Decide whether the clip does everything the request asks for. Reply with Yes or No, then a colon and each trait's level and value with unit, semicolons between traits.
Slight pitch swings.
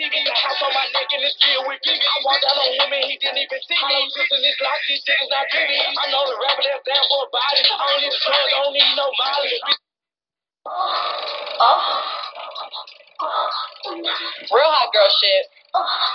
Yes: narrow, 0.9 semitones